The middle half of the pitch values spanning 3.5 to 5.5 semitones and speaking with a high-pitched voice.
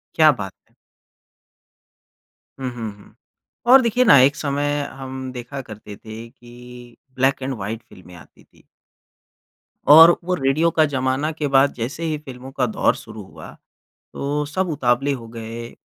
No: average, 3.8 semitones; low, 130 Hz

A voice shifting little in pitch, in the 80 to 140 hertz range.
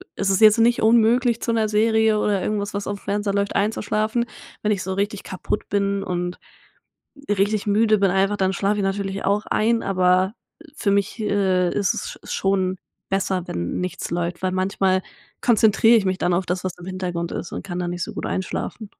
No: narrow, 2.3 semitones; high, 200 Hz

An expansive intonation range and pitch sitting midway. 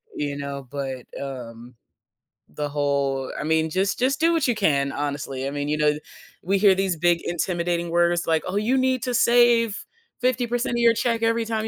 Yes: wide, 8.3 semitones; medium, 175 Hz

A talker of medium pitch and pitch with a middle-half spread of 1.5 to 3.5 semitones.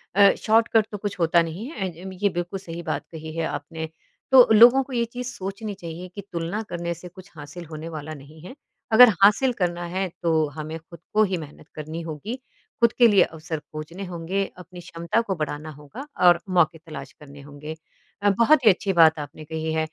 No: medium, 175 Hz; average, 4.2 semitones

